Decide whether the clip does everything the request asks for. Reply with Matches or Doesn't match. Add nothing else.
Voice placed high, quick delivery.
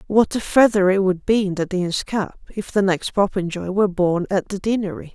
Matches